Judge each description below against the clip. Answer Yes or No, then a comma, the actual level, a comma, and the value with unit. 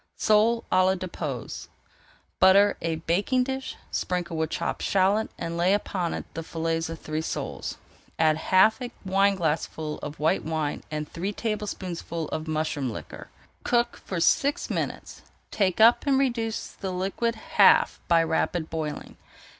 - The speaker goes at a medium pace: Yes, average, 155 wpm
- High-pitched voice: No, medium, 180 Hz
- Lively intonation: No, average, 4.7 semitones